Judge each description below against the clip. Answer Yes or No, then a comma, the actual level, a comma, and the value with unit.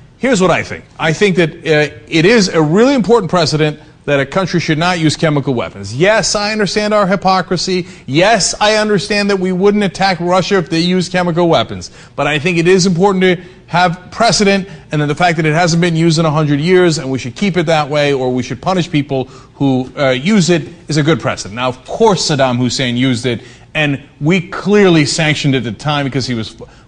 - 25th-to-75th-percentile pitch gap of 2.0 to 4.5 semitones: No, average, 4.9 semitones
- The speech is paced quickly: Yes, fast, 220 wpm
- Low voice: No, medium, 165 Hz